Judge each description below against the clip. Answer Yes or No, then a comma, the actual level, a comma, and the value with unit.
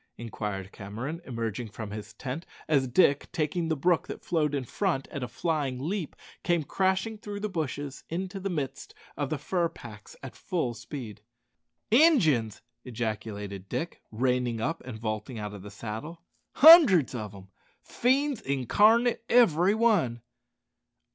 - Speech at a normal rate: Yes, average, 150 wpm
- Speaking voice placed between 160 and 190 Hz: No, medium, 140 Hz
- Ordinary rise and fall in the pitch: No, wide, 8.0 semitones